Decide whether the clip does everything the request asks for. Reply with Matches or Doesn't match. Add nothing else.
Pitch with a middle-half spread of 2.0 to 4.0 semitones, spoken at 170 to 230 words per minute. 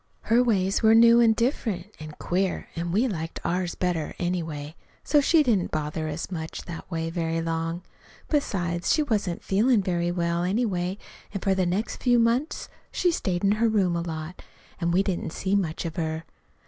Doesn't match